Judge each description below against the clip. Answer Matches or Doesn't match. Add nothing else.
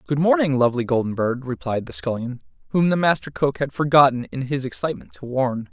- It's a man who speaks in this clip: Matches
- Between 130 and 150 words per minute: Doesn't match